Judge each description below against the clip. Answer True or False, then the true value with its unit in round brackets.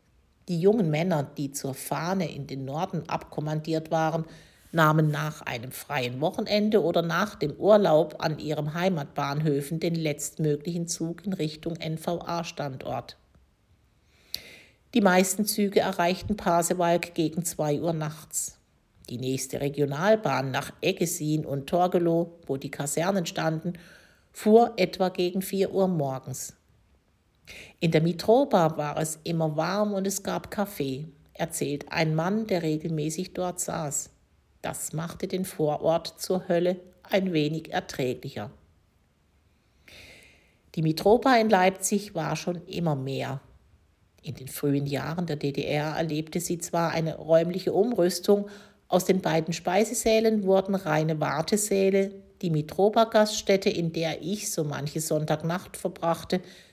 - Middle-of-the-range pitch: True (165 Hz)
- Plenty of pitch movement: False (3.7 semitones)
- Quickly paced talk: False (125 wpm)